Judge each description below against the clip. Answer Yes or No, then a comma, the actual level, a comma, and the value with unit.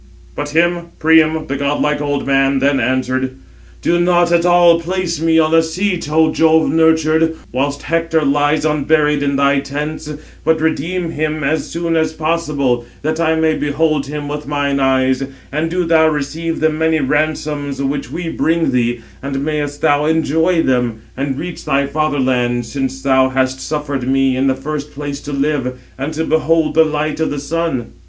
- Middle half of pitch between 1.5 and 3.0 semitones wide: Yes, average, 2.7 semitones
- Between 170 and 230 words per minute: Yes, average, 175 wpm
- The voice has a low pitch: No, medium, 150 Hz